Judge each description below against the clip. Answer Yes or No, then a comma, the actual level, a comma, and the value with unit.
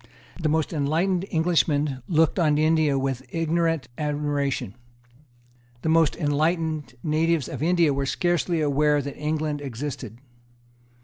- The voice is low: No, medium, 155 Hz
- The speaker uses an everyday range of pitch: No, narrow, 2.3 semitones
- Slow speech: Yes, slow, 120 wpm